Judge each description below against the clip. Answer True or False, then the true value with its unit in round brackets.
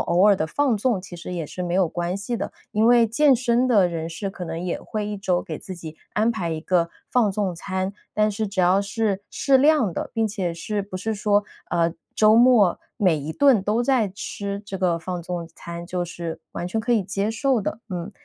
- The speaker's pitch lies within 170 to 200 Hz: True (195 Hz)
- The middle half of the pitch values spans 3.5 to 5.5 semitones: True (3.9 semitones)